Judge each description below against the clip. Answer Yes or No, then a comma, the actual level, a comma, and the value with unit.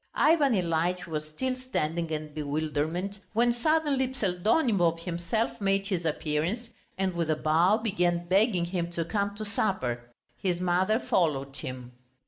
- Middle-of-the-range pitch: Yes, medium, 180 Hz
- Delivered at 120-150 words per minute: Yes, average, 140 wpm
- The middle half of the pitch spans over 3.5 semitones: Yes, average, 5.2 semitones